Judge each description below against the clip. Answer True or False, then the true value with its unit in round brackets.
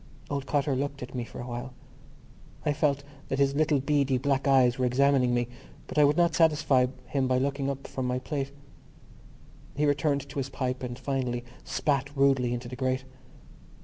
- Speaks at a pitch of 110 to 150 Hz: True (135 Hz)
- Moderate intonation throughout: False (1.9 semitones)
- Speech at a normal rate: True (185 wpm)